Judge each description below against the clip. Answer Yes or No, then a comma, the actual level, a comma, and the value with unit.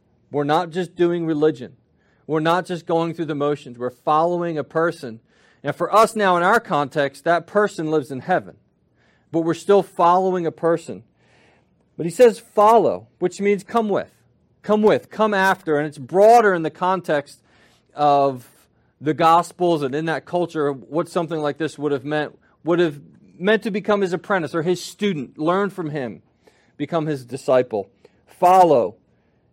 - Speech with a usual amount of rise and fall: Yes, average, 4.0 semitones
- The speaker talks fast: No, average, 170 wpm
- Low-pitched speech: No, medium, 165 Hz